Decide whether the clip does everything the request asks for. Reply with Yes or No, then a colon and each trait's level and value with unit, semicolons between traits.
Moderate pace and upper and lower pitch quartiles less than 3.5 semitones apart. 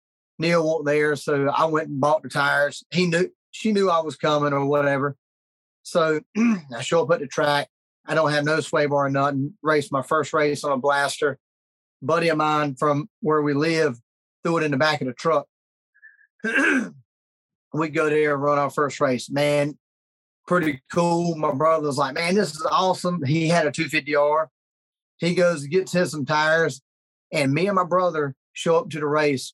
Yes: average, 195 wpm; average, 2.8 semitones